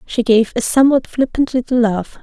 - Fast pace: No, average, 190 wpm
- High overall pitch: Yes, high, 240 Hz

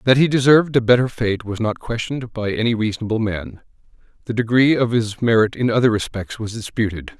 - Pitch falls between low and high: No, low, 115 Hz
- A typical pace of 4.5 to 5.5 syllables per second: No, 6.0 syllables/s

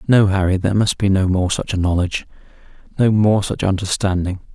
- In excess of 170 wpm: No, average, 160 wpm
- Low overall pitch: Yes, very low, 95 Hz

